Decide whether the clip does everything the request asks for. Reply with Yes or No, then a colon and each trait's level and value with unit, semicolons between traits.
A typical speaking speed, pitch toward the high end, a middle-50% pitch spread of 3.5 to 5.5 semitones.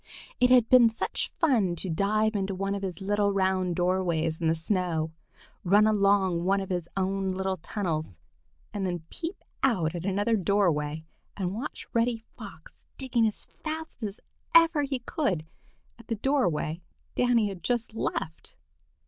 Yes: average, 155 wpm; high, 195 Hz; average, 4.3 semitones